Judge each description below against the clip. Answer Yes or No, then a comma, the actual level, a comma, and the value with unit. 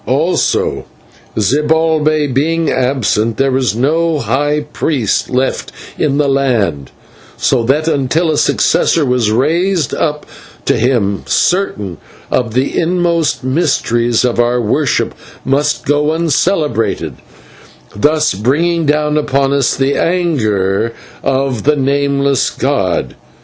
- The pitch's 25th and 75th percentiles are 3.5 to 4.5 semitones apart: Yes, average, 3.9 semitones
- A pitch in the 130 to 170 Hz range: Yes, medium, 140 Hz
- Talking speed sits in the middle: No, slow, 115 wpm